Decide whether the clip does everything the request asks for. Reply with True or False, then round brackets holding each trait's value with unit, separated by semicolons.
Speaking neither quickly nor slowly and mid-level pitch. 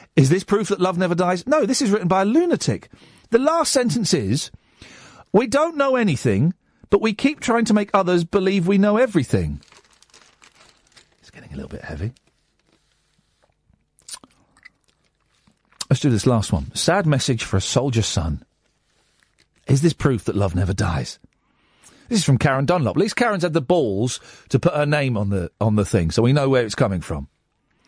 True (180 wpm; 150 Hz)